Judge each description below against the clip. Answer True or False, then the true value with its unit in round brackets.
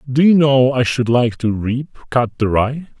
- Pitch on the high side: False (125 Hz)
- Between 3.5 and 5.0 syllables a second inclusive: True (4.9 syllables/s)